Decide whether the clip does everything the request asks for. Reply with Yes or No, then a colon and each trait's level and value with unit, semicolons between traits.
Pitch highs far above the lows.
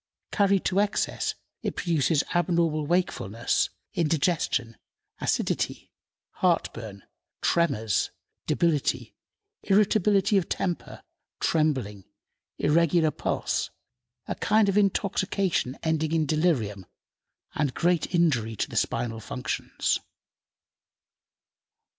Yes: wide, 5.8 semitones